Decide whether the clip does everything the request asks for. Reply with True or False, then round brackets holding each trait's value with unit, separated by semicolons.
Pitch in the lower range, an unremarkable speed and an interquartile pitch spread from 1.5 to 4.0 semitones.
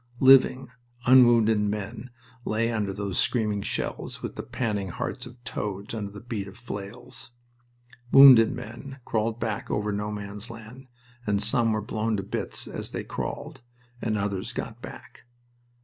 True (110 Hz; 150 wpm; 2.7 semitones)